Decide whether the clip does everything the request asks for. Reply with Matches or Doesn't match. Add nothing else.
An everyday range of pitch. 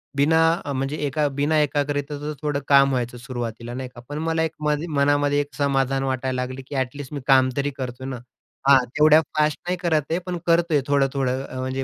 Doesn't match